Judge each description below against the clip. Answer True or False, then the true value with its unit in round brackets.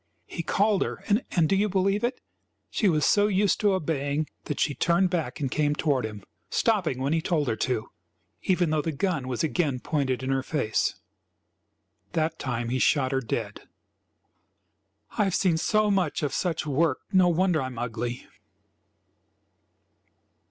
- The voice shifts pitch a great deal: True (5.8 semitones)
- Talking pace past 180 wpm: False (165 wpm)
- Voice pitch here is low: False (155 Hz)